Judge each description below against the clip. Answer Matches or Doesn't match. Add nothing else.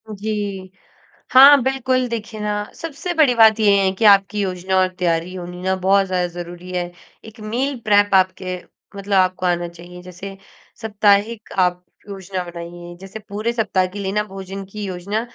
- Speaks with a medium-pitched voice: Doesn't match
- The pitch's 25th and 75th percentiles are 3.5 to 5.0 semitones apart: Doesn't match